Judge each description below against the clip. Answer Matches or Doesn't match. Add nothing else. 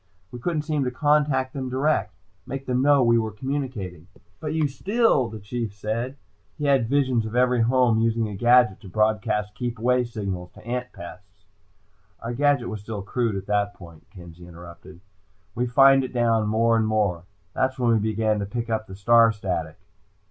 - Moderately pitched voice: Doesn't match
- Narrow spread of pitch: Doesn't match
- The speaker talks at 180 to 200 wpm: Matches